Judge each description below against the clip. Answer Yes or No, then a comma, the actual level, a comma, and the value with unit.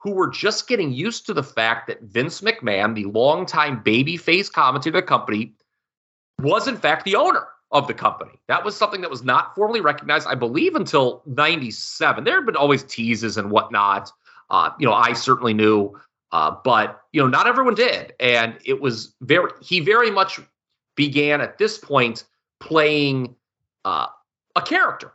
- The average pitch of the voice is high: No, low, 135 Hz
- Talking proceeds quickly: No, average, 170 wpm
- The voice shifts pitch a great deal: Yes, wide, 7.5 semitones